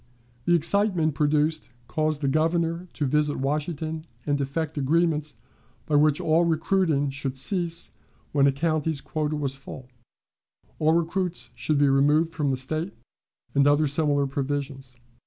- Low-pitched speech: No, medium, 150 Hz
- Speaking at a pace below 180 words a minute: Yes, average, 140 wpm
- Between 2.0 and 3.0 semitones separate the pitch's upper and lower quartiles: Yes, narrow, 2.5 semitones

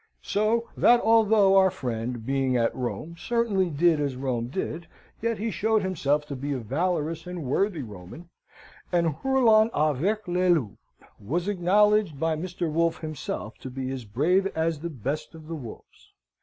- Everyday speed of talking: Yes, average, 165 wpm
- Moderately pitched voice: Yes, medium, 165 Hz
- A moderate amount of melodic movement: No, wide, 6.0 semitones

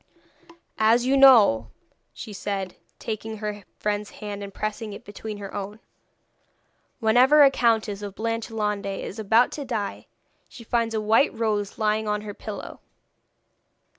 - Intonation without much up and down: Yes, narrow, 1.8 semitones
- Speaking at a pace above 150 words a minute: No, average, 140 wpm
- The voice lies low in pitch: No, high, 215 Hz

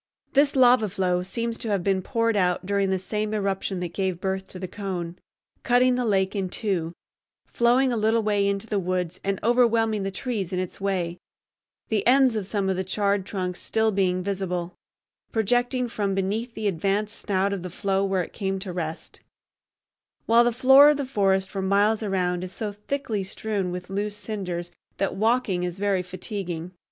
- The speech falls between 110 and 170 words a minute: No, average, 185 wpm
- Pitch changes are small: No, average, 3.1 semitones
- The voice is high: Yes, high, 195 Hz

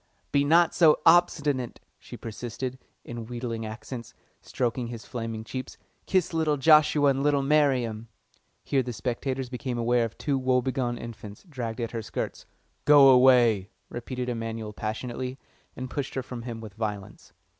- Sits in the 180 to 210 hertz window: No, low, 125 Hz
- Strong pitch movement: No, average, 2.9 semitones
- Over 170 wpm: No, average, 150 wpm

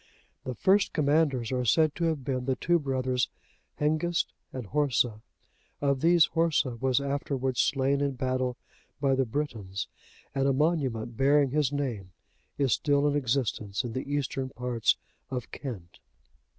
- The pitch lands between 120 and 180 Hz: Yes, low, 135 Hz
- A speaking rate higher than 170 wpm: No, average, 150 wpm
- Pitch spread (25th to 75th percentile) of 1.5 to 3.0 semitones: Yes, average, 2.7 semitones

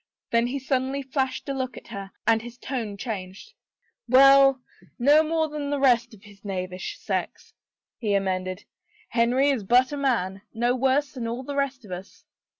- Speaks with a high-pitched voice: Yes, very high, 250 Hz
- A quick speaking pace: No, average, 185 wpm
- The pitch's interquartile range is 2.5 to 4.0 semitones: No, average, 4.9 semitones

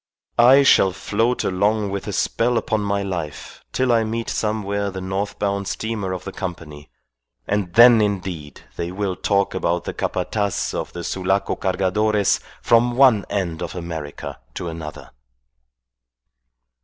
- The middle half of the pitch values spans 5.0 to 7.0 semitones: No, average, 2.9 semitones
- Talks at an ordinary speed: Yes, average, 145 wpm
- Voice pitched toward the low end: Yes, low, 100 Hz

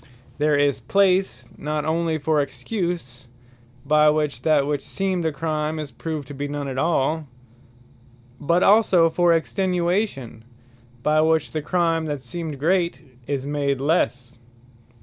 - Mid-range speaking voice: Yes, medium, 155 Hz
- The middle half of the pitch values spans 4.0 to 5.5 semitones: No, average, 3.0 semitones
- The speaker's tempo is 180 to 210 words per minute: No, average, 140 wpm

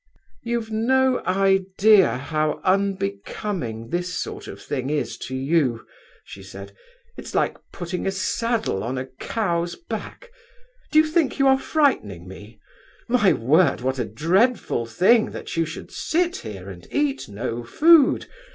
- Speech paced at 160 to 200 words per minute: No, average, 145 wpm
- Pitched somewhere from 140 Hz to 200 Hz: Yes, medium, 185 Hz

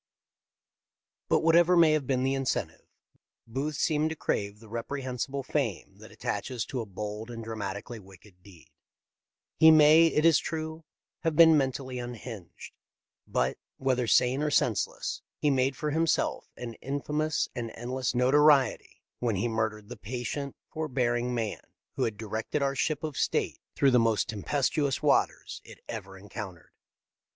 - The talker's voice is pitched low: Yes, low, 130 Hz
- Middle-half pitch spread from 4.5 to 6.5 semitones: Yes, average, 4.8 semitones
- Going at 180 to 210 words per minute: No, average, 155 wpm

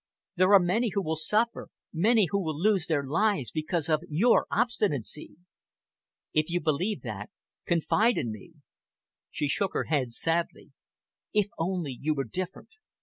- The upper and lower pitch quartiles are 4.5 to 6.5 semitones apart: Yes, average, 4.8 semitones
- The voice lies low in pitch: No, medium, 170 Hz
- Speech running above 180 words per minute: No, average, 150 wpm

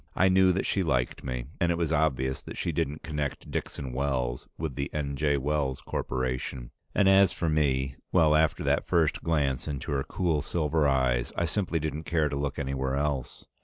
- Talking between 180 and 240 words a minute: Yes, average, 195 wpm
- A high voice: No, very low, 75 Hz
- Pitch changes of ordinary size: Yes, average, 3.3 semitones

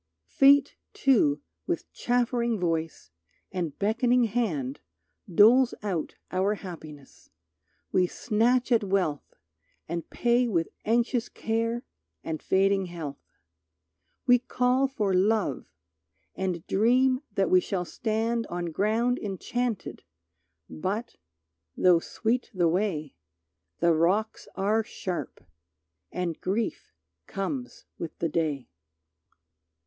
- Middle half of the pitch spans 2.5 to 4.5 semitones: No, wide, 5.6 semitones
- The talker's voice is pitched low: No, high, 200 Hz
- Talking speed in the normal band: No, slow, 105 wpm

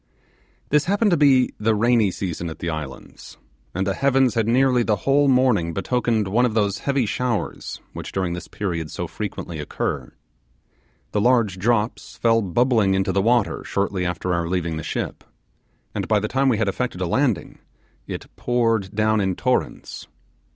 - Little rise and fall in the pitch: No, average, 4.8 semitones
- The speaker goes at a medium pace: Yes, average, 170 wpm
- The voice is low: Yes, low, 110 Hz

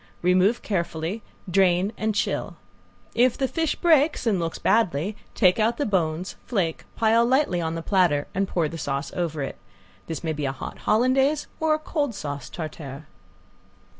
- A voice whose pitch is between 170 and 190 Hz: Yes, medium, 185 Hz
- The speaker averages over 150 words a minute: Yes, average, 170 wpm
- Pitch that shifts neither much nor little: No, wide, 6.5 semitones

